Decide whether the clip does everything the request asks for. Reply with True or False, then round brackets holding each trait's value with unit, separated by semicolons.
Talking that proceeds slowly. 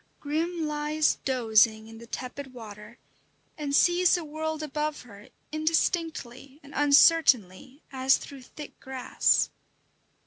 True (115 wpm)